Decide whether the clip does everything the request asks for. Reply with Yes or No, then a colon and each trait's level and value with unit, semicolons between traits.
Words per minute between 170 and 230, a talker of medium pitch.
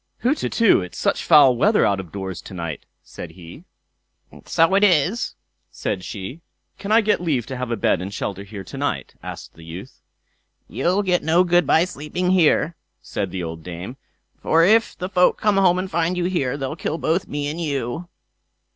Yes: average, 190 wpm; medium, 155 Hz